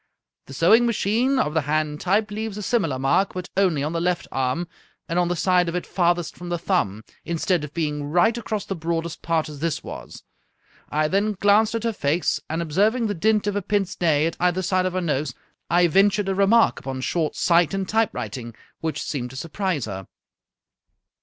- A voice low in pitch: No, medium, 175 Hz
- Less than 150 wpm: No, fast, 205 wpm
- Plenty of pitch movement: No, average, 4.5 semitones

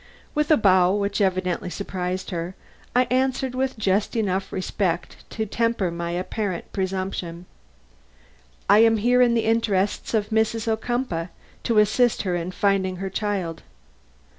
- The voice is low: No, high, 200 Hz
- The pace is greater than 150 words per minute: No, average, 140 wpm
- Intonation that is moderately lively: Yes, average, 3.6 semitones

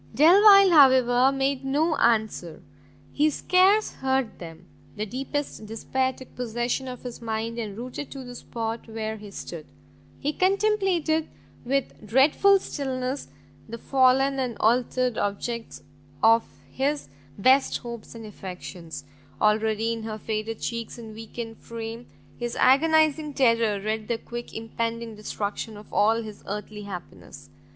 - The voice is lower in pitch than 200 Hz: No, high, 235 Hz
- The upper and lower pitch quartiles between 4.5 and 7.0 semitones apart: No, average, 3.7 semitones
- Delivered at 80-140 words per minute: Yes, slow, 135 wpm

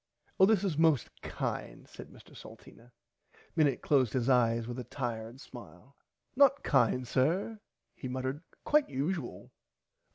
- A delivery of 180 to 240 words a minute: No, slow, 135 wpm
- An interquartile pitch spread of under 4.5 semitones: No, average, 5.2 semitones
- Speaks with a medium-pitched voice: No, low, 130 Hz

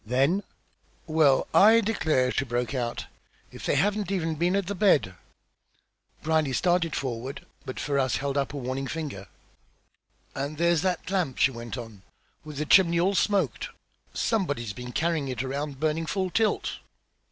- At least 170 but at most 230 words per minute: No, average, 155 wpm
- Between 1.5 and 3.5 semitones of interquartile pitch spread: No, average, 5.2 semitones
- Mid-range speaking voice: Yes, medium, 150 Hz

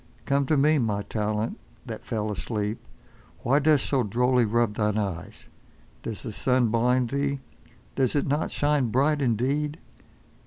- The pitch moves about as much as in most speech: Yes, average, 4.4 semitones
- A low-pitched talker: Yes, low, 125 Hz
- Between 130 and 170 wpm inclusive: Yes, average, 150 wpm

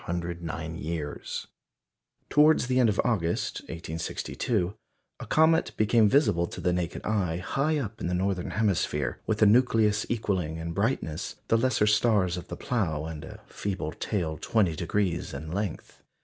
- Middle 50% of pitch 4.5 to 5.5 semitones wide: Yes, average, 4.9 semitones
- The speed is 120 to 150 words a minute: Yes, average, 145 wpm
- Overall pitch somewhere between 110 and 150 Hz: No, low, 100 Hz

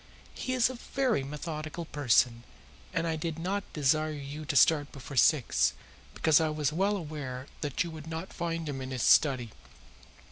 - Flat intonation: No, average, 3.1 semitones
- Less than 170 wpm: No, average, 175 wpm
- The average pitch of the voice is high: No, medium, 155 Hz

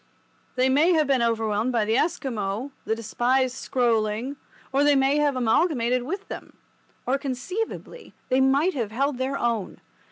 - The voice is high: Yes, very high, 260 Hz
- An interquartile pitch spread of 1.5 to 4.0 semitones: Yes, average, 3.5 semitones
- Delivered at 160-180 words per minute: No, average, 140 wpm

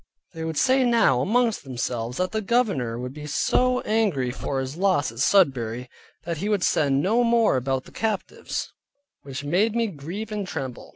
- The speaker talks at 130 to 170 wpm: No, average, 180 wpm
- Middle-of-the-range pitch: Yes, medium, 165 Hz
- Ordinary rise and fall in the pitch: No, wide, 8.6 semitones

